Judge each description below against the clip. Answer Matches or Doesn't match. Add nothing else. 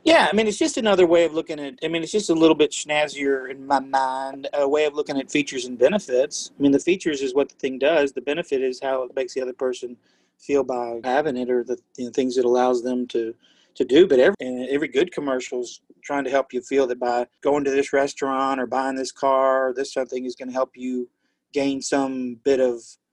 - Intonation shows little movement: Matches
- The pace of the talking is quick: Matches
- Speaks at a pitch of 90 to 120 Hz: Doesn't match